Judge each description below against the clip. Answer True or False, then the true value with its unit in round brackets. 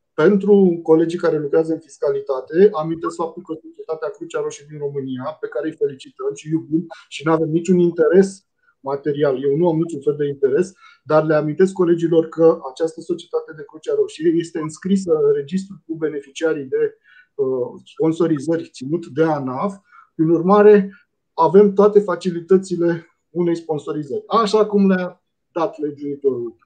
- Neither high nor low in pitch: True (175 Hz)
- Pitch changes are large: False (4.4 semitones)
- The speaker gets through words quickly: False (150 wpm)